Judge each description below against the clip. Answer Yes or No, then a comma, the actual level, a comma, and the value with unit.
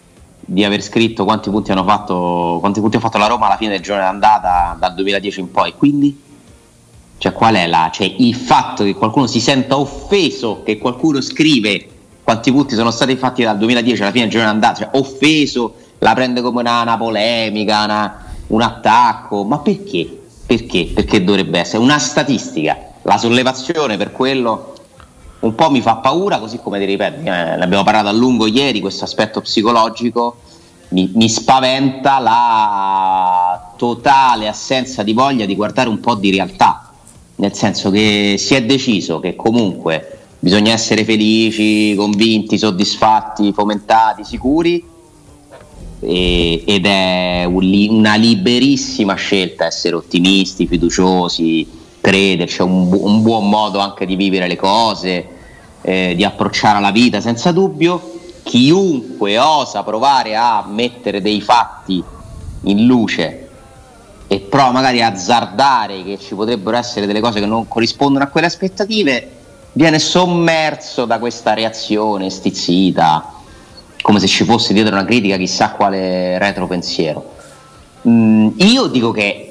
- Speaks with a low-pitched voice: Yes, low, 110 Hz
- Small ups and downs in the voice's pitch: No, average, 3.8 semitones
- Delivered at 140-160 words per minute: Yes, average, 145 wpm